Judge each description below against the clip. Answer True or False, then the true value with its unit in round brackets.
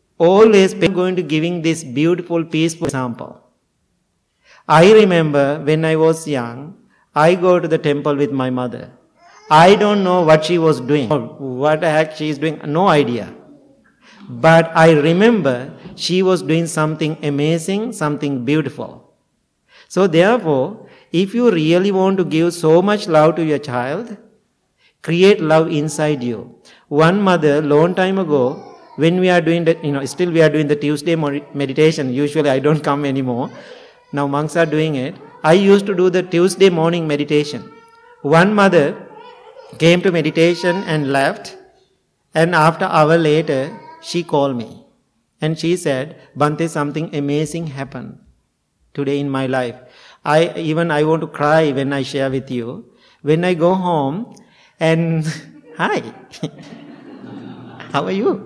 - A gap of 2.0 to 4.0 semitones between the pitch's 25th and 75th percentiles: True (3.7 semitones)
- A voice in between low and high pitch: True (160 Hz)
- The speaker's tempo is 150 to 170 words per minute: True (155 wpm)